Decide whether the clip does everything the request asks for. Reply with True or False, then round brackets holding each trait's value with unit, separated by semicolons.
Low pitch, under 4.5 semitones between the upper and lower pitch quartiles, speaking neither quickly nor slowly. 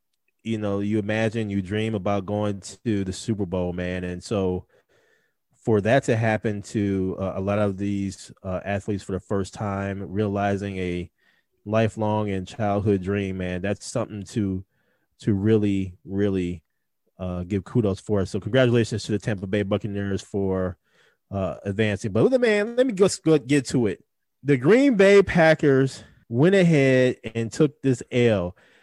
True (105 Hz; 2.9 semitones; 160 wpm)